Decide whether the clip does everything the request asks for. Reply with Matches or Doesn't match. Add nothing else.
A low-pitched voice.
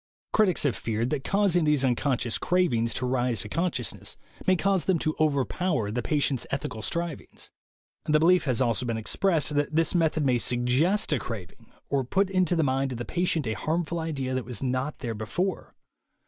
Doesn't match